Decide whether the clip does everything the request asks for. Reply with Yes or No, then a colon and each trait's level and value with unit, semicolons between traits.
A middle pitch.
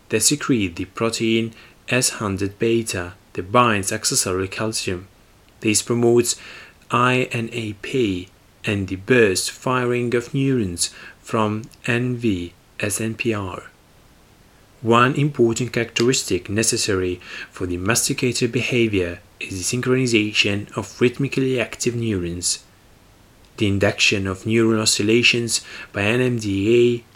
No: low, 115 Hz